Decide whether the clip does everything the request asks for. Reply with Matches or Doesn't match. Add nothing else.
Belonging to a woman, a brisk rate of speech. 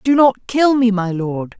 Matches